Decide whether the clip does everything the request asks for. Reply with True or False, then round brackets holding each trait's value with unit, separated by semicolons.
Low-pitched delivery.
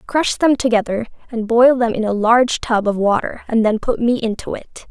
False (230 Hz)